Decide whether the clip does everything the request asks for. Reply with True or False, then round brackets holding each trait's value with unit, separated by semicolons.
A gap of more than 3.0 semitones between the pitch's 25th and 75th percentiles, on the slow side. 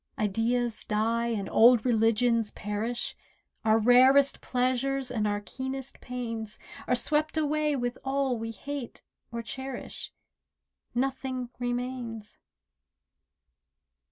False (2.7 semitones; 100 wpm)